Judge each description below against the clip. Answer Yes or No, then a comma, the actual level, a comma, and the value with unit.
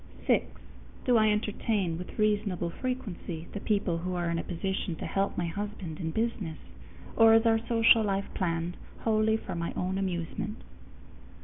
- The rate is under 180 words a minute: Yes, average, 165 wpm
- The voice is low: No, high, 195 Hz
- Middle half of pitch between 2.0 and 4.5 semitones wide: Yes, average, 4.0 semitones